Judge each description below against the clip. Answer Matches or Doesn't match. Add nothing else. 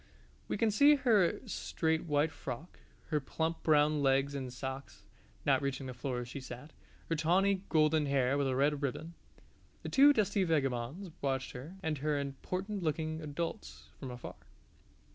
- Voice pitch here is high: Doesn't match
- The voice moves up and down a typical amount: Matches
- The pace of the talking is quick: Doesn't match